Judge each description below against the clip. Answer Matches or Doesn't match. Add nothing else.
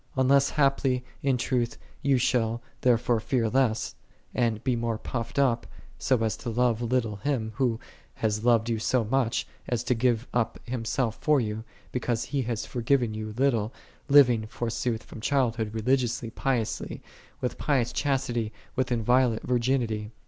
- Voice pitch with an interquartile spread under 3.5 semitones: Matches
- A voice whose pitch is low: Matches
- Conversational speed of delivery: Matches